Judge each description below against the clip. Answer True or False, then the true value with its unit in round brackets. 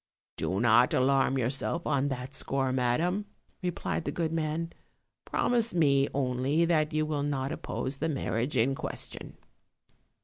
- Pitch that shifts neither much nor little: True (3.7 semitones)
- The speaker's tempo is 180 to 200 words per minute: False (140 wpm)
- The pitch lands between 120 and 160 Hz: True (140 Hz)